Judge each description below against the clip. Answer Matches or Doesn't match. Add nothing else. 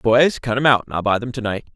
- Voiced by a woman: Doesn't match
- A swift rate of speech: Matches